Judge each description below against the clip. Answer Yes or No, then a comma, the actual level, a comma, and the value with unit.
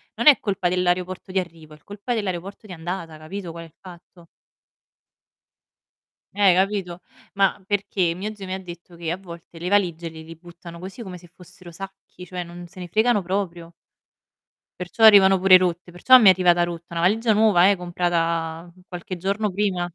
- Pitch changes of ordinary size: No, narrow, 2.3 semitones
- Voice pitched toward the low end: No, medium, 180 Hz